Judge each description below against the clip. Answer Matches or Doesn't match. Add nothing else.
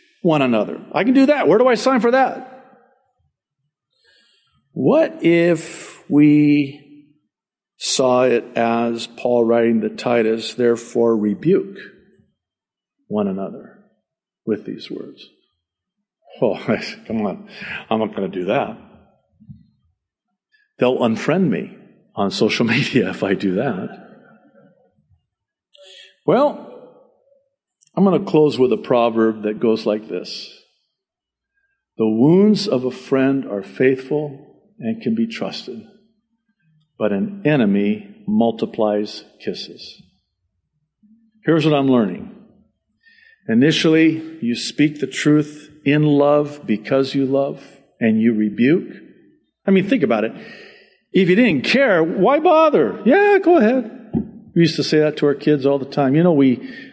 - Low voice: Doesn't match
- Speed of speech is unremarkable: Doesn't match